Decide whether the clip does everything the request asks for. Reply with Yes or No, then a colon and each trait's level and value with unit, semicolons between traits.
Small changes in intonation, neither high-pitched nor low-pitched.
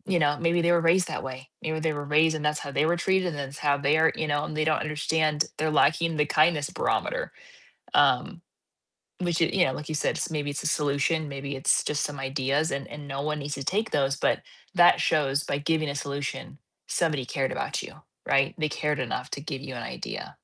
Yes: narrow, 2.1 semitones; medium, 150 Hz